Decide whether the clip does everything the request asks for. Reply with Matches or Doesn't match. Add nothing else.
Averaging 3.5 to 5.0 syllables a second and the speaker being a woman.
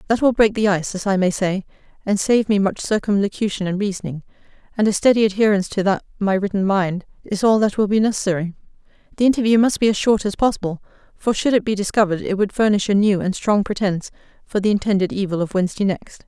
Doesn't match